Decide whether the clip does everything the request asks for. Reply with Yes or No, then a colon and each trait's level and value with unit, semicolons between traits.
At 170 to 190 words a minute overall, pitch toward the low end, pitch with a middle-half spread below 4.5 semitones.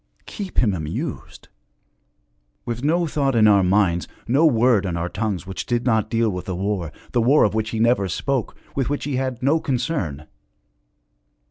No: average, 175 wpm; low, 115 Hz; wide, 5.6 semitones